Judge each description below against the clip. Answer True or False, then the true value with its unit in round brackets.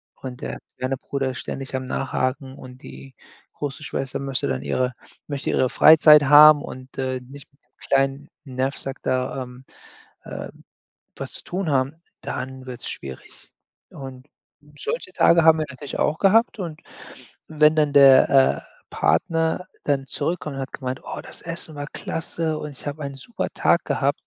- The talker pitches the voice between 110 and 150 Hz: True (135 Hz)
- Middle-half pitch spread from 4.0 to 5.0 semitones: False (2.6 semitones)